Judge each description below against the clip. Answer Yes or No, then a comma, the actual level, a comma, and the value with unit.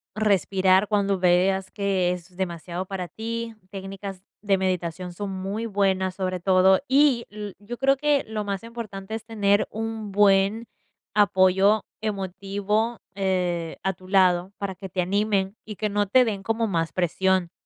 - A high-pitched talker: Yes, high, 195 Hz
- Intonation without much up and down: Yes, narrow, 2.3 semitones